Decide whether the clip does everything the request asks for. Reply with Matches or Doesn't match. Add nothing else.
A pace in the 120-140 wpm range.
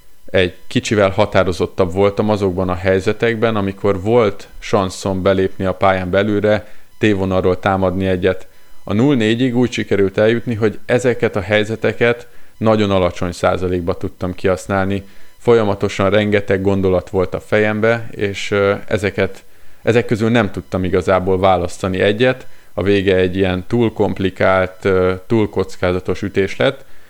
Matches